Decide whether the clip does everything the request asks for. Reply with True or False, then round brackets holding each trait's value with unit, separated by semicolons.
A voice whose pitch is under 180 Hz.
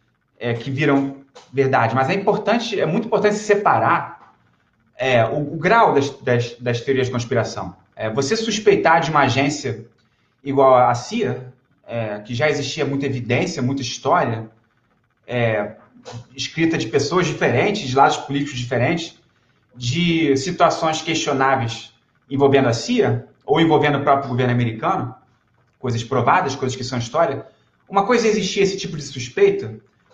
True (135 Hz)